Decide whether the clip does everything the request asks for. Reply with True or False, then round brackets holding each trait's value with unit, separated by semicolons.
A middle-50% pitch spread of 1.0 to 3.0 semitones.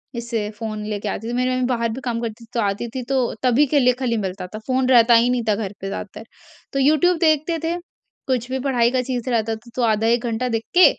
True (2.5 semitones)